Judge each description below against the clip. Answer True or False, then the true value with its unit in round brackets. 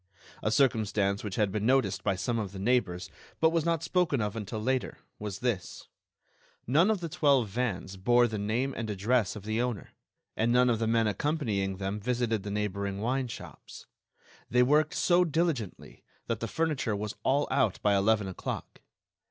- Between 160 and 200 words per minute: True (180 wpm)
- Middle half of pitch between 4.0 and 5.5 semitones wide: True (4.4 semitones)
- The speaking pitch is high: False (115 Hz)